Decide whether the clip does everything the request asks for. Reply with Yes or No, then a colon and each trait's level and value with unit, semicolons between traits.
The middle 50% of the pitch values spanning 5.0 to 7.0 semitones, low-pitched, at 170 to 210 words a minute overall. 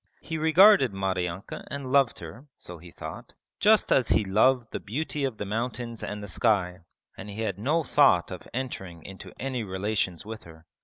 Yes: wide, 5.6 semitones; low, 110 Hz; average, 185 wpm